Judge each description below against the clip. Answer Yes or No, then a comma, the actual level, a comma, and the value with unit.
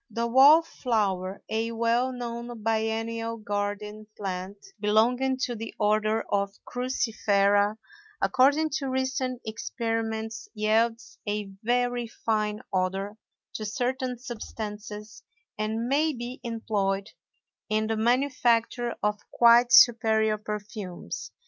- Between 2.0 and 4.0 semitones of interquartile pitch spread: Yes, narrow, 2.4 semitones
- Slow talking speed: Yes, slow, 105 wpm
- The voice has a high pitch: Yes, high, 225 Hz